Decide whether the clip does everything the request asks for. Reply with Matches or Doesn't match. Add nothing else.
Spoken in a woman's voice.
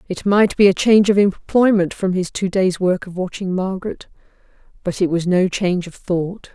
Matches